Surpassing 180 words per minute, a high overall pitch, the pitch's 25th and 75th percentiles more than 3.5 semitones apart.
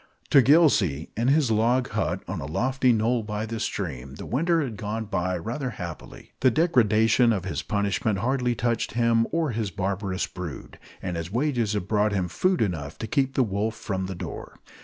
No: average, 190 wpm; low, 110 Hz; average, 4.6 semitones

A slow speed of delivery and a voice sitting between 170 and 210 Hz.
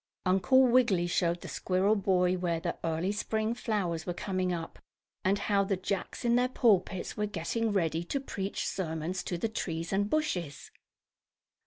No: average, 165 wpm; high, 190 Hz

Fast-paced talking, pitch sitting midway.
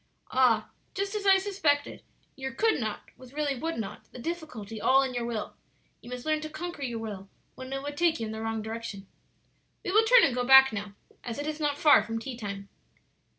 No: fast, 220 wpm; very high, 265 Hz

